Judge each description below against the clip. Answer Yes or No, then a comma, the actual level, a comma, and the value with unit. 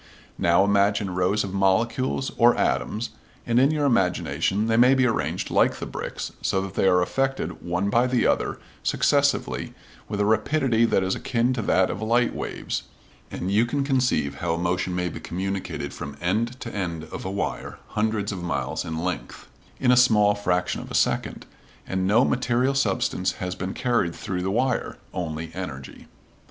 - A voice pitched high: No, low, 100 Hz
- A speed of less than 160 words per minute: No, average, 180 wpm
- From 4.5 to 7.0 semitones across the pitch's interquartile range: Yes, average, 4.9 semitones